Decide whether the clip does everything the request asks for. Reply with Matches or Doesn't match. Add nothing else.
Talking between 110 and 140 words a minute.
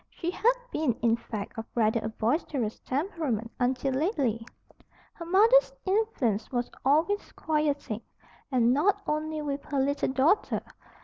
Matches